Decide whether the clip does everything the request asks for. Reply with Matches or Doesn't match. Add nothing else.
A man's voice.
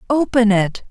Doesn't match